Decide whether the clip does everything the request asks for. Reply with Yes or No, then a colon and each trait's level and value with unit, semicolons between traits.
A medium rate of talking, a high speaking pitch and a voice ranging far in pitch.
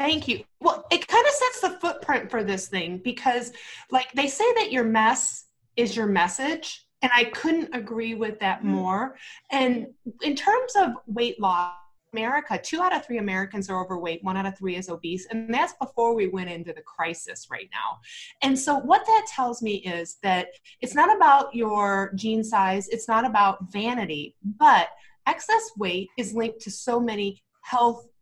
Yes: average, 185 wpm; high, 230 Hz; wide, 6.3 semitones